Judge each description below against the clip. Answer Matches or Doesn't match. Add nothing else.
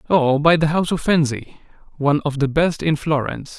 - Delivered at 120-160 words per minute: Doesn't match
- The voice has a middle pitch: Matches